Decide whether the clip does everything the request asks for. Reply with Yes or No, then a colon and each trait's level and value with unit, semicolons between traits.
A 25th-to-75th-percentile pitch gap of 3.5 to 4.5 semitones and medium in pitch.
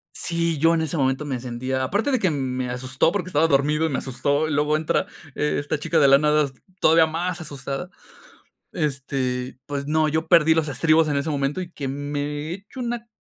No: average, 2.9 semitones; medium, 150 Hz